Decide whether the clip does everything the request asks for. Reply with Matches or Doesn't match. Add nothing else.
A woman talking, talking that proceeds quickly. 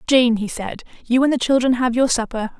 Matches